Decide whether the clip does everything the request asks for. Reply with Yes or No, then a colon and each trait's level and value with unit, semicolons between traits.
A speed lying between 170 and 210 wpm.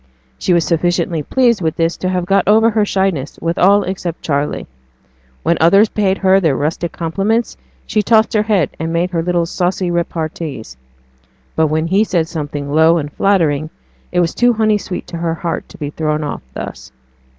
Yes: average, 185 wpm